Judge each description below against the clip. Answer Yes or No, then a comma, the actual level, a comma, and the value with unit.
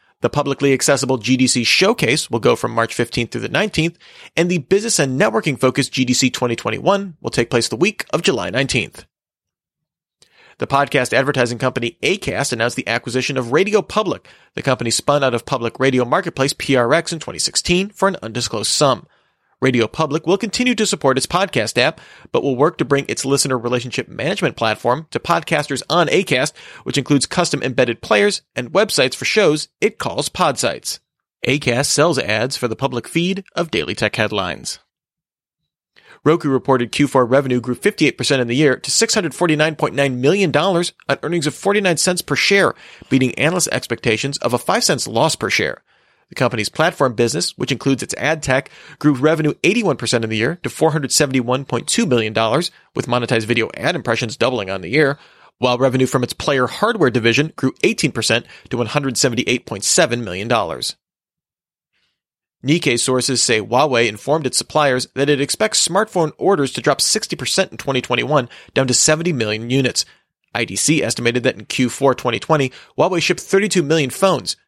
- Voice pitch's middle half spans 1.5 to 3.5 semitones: No, average, 4.5 semitones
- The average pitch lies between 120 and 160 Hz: Yes, low, 135 Hz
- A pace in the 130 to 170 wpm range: Yes, average, 165 wpm